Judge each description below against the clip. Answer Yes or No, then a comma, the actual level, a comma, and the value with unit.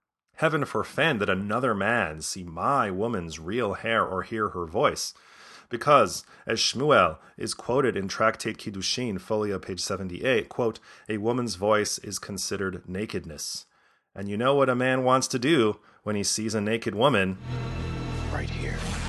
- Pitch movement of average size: Yes, average, 3.9 semitones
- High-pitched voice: No, low, 105 Hz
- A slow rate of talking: No, average, 155 wpm